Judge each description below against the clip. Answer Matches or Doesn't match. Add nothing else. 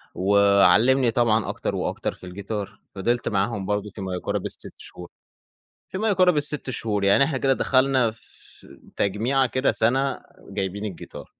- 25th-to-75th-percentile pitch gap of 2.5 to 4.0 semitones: Doesn't match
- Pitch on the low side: Matches